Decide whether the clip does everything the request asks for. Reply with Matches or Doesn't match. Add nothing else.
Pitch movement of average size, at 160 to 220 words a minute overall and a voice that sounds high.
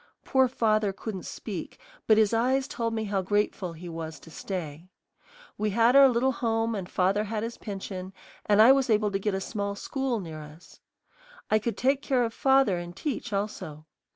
Matches